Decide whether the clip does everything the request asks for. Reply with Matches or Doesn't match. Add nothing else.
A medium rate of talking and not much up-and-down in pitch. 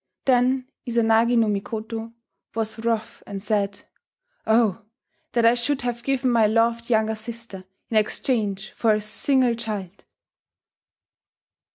Doesn't match